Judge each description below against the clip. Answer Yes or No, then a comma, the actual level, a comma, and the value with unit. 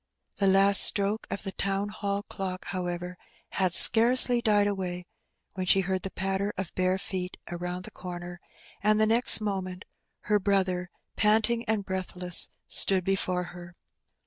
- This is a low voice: No, high, 190 Hz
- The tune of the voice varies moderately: No, narrow, 2.1 semitones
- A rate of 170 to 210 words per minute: No, average, 150 wpm